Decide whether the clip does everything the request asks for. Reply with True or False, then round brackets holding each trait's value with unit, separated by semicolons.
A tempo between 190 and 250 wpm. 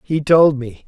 True (205 wpm)